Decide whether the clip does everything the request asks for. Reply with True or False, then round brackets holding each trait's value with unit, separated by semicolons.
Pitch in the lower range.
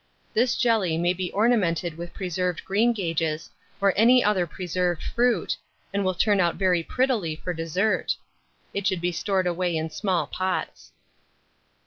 False (185 Hz)